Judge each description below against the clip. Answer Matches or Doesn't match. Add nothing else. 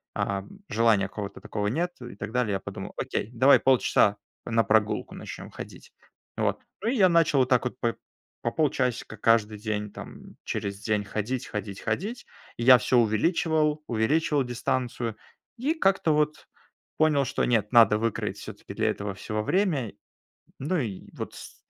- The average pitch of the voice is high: Doesn't match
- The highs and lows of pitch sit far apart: Matches